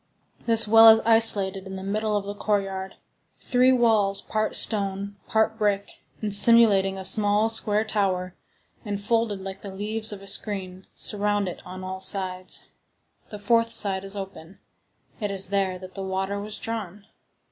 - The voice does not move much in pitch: Yes, narrow, 2.1 semitones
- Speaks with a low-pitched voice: No, high, 200 Hz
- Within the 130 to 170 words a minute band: Yes, average, 165 wpm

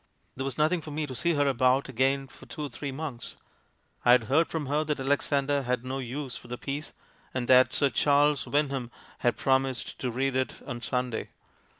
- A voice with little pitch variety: Yes, narrow, 2.3 semitones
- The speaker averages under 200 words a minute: No, fast, 205 wpm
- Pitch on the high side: No, low, 135 Hz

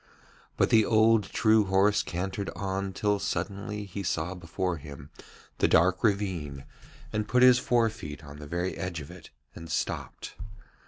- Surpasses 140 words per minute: Yes, average, 160 wpm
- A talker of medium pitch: No, very low, 95 Hz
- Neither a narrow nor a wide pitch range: Yes, average, 3.8 semitones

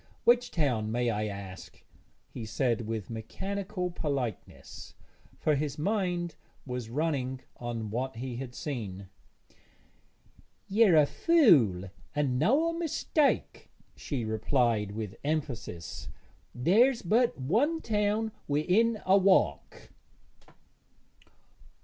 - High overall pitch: No, medium, 140 Hz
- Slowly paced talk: Yes, slow, 100 wpm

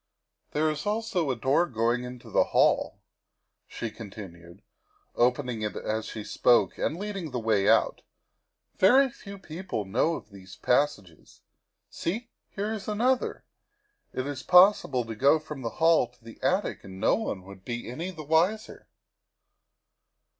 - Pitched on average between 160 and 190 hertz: No, low, 135 Hz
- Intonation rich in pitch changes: Yes, wide, 8.4 semitones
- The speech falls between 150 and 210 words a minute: Yes, average, 160 wpm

